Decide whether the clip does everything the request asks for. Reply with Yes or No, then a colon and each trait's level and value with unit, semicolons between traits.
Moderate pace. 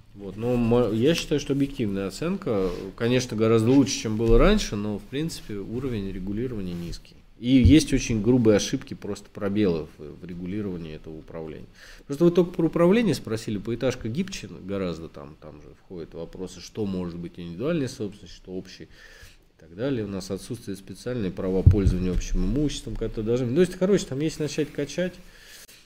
No: fast, 165 wpm